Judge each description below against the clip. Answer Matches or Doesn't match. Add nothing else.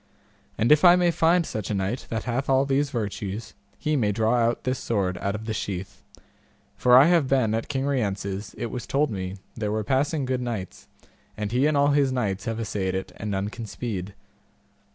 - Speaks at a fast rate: Matches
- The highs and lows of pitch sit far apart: Doesn't match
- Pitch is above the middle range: Doesn't match